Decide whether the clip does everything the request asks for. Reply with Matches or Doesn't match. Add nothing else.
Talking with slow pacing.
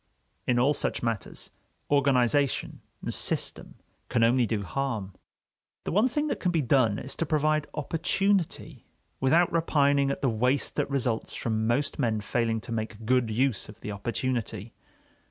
Doesn't match